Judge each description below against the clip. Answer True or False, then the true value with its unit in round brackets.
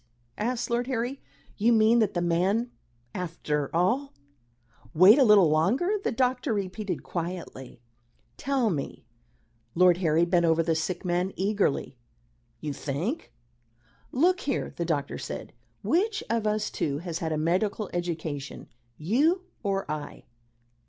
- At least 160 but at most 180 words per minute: False (140 wpm)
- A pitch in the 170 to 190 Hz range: True (185 Hz)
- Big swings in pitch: True (6.4 semitones)